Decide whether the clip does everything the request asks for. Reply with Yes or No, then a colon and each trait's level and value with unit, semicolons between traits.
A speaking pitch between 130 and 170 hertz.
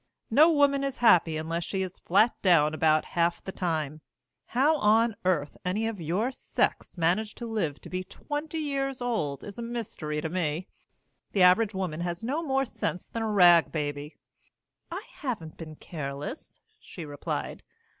No: medium, 185 Hz